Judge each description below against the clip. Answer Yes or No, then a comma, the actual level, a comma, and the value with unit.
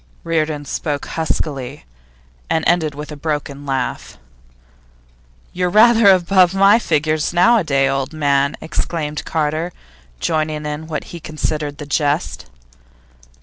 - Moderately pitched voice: Yes, medium, 155 Hz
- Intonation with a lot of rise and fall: No, average, 2.7 semitones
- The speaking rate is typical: No, slow, 115 wpm